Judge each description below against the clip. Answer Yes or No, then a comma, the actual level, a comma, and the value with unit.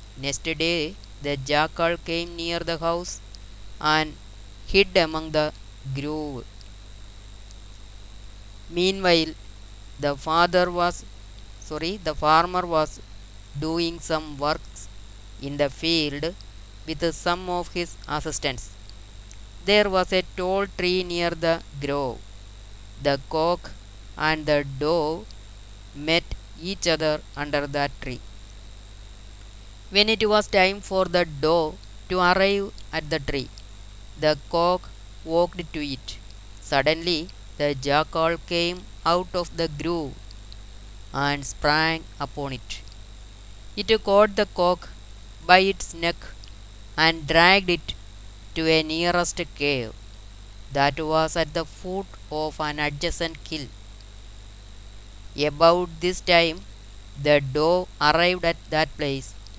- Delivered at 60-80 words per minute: No, average, 115 wpm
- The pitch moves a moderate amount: No, wide, 8.5 semitones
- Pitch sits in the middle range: Yes, medium, 150 Hz